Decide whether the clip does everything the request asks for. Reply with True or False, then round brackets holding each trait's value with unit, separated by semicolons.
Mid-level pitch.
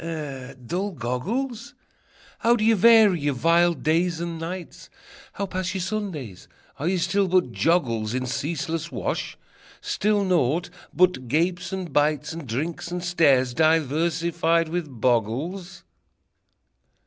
True (165 Hz)